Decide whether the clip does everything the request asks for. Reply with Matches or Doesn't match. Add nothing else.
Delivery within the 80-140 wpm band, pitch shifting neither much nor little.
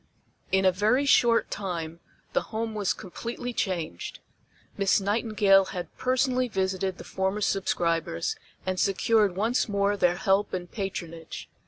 Matches